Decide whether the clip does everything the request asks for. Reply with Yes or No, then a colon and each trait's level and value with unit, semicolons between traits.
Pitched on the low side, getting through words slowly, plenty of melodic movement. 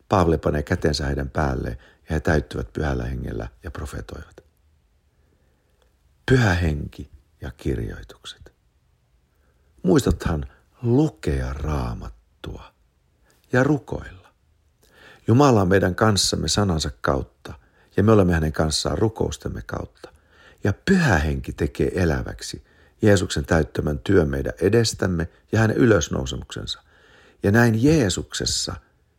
Yes: very low, 80 Hz; slow, 100 wpm; wide, 5.8 semitones